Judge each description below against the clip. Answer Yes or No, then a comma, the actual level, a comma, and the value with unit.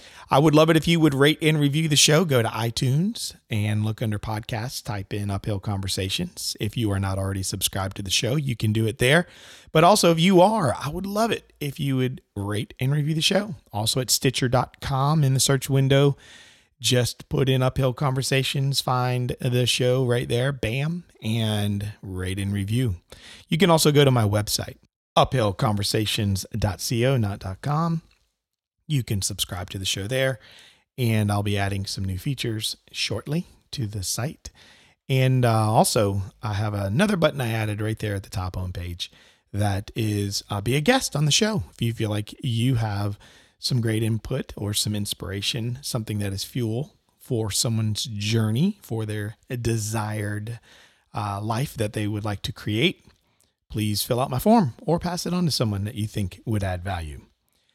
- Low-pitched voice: Yes, low, 115 Hz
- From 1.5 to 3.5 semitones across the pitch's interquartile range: No, average, 4.8 semitones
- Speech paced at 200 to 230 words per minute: No, average, 185 wpm